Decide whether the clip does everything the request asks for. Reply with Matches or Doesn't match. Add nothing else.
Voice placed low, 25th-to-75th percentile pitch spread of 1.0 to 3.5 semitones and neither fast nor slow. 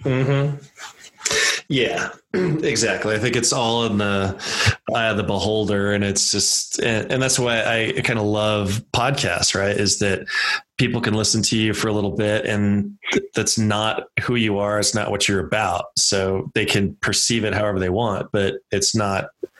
Matches